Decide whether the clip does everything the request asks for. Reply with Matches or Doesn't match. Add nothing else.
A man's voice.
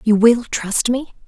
Doesn't match